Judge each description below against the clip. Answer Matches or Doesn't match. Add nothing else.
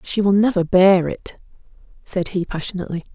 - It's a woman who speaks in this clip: Matches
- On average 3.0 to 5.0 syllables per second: Doesn't match